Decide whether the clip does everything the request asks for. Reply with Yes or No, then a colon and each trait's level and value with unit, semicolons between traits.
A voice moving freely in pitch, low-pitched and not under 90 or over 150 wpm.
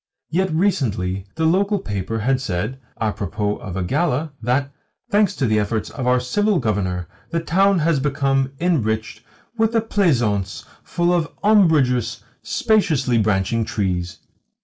Yes: wide, 8.2 semitones; low, 130 Hz; average, 140 wpm